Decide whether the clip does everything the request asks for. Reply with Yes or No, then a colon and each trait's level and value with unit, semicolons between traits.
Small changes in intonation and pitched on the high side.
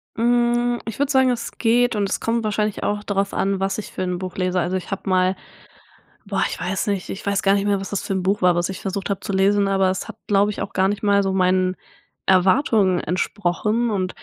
Yes: narrow, 2.2 semitones; high, 195 Hz